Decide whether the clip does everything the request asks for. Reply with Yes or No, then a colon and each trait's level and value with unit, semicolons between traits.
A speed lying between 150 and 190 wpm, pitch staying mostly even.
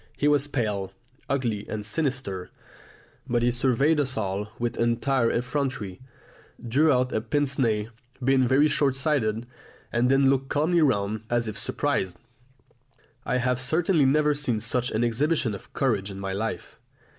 No: average, 155 wpm; average, 4.2 semitones